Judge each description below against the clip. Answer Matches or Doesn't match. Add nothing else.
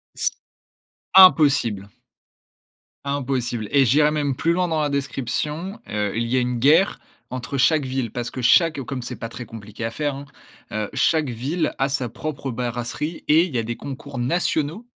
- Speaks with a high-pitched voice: Doesn't match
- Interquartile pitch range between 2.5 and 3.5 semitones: Doesn't match